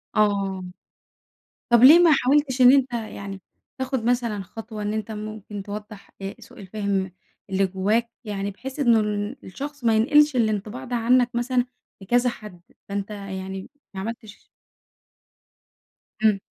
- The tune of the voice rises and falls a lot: No, average, 3.7 semitones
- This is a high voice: Yes, high, 215 Hz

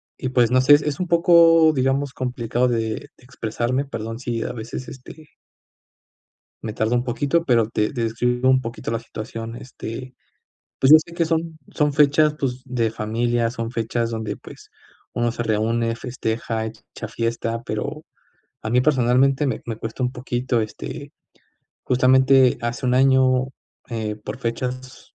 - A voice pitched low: Yes, low, 125 Hz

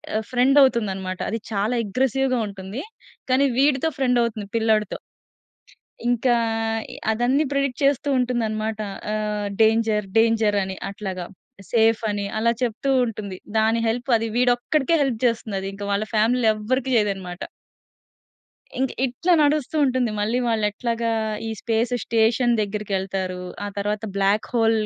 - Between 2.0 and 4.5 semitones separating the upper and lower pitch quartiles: Yes, average, 3.0 semitones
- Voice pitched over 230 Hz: No, high, 225 Hz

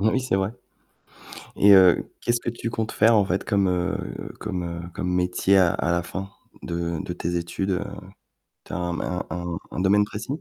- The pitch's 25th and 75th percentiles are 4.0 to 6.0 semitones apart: No, average, 2.8 semitones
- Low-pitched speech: Yes, very low, 95 Hz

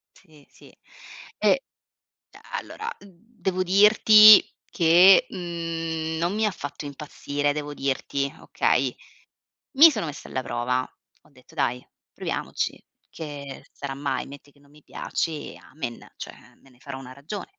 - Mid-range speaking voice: Yes, medium, 150 Hz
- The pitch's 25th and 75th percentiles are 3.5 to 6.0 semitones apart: Yes, average, 4.8 semitones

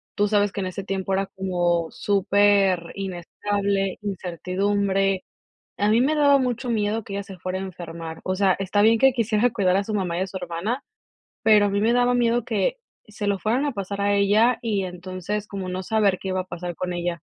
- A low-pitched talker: No, high, 200 Hz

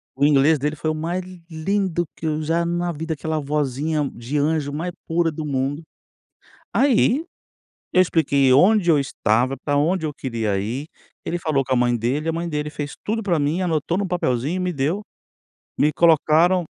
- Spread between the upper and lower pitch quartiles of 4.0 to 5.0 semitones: No, average, 3.4 semitones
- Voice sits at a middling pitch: Yes, medium, 155 Hz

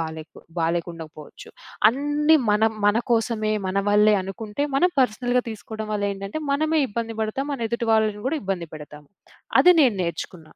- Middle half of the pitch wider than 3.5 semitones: Yes, average, 4.1 semitones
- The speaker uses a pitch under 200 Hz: No, high, 215 Hz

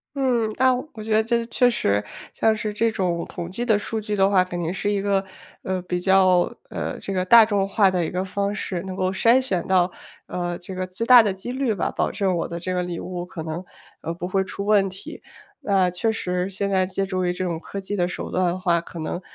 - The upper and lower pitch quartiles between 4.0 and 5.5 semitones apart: No, average, 2.9 semitones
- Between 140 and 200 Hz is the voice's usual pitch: Yes, high, 190 Hz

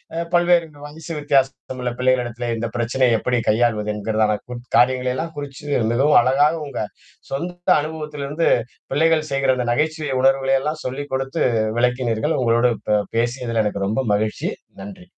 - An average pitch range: Yes, average, 3.8 semitones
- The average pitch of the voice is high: No, low, 130 Hz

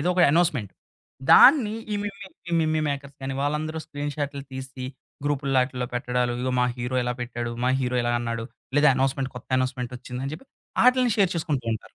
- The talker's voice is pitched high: No, low, 135 Hz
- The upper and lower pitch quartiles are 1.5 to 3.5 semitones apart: No, average, 3.9 semitones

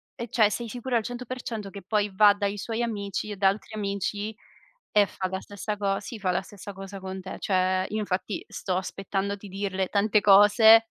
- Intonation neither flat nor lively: No, narrow, 1.9 semitones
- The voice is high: Yes, high, 205 Hz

